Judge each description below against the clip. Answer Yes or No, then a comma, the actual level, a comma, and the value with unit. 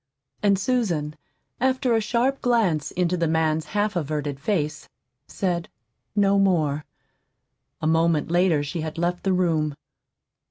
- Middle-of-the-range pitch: Yes, medium, 175 Hz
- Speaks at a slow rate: Yes, slow, 130 wpm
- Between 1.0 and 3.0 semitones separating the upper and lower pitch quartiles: No, average, 4.8 semitones